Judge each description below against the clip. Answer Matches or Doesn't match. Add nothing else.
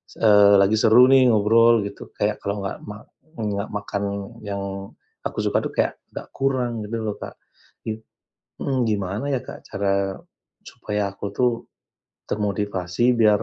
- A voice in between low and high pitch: Doesn't match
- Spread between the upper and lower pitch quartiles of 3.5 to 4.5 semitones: Doesn't match